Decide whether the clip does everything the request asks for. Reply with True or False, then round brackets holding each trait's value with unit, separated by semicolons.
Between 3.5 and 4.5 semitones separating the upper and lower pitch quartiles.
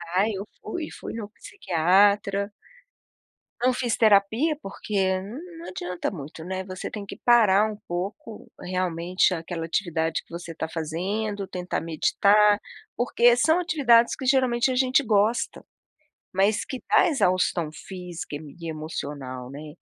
False (5.1 semitones)